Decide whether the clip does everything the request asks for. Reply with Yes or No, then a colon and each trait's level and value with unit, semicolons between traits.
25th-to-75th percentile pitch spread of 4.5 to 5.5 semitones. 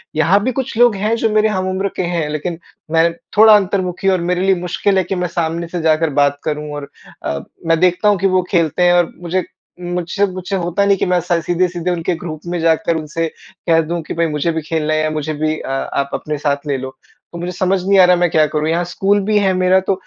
No: average, 2.9 semitones